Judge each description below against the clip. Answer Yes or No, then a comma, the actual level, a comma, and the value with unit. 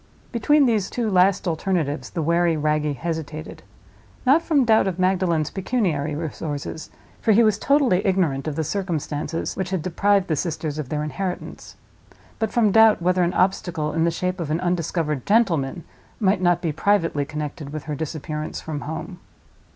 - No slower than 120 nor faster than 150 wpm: No, average, 160 wpm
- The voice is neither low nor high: Yes, medium, 170 Hz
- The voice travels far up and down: No, average, 4.2 semitones